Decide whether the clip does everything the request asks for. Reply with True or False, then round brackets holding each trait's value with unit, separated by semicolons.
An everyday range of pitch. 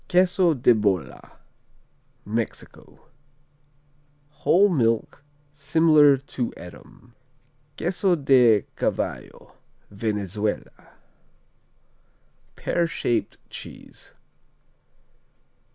False (7.1 semitones)